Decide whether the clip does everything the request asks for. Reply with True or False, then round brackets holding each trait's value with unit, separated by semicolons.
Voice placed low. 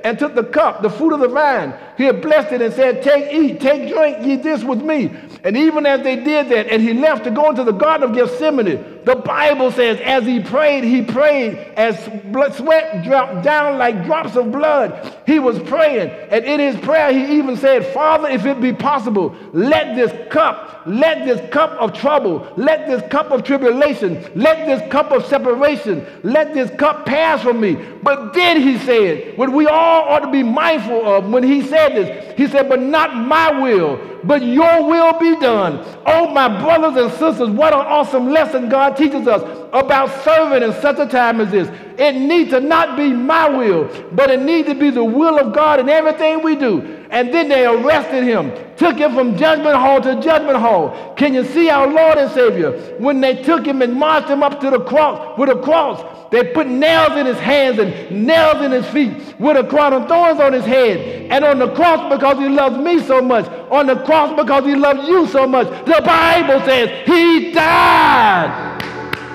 False (280 Hz)